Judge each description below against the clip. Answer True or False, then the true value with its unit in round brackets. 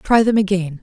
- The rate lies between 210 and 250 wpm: True (220 wpm)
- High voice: True (195 Hz)